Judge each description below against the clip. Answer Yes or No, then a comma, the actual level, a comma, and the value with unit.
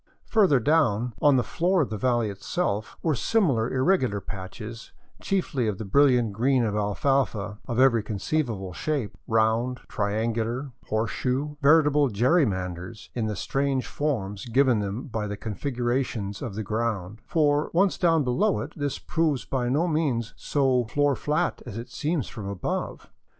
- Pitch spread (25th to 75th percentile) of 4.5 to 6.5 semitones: Yes, average, 5.1 semitones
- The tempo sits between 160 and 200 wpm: Yes, average, 165 wpm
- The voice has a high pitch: No, low, 125 Hz